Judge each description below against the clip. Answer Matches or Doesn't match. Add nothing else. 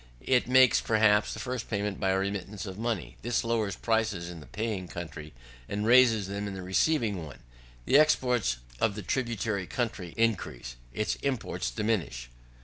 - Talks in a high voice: Doesn't match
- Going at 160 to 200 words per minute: Matches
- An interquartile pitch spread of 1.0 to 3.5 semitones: Doesn't match